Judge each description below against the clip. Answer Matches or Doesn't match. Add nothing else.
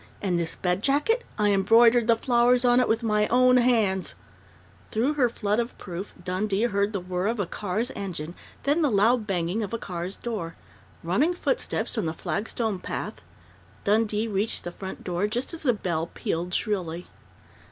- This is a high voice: Matches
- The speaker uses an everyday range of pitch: Matches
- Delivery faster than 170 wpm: Matches